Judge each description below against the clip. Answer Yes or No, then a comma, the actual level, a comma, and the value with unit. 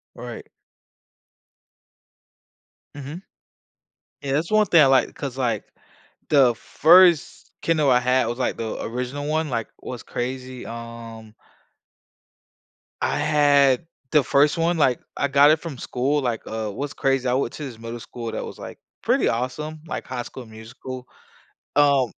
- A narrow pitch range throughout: No, average, 3.4 semitones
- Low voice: Yes, low, 130 Hz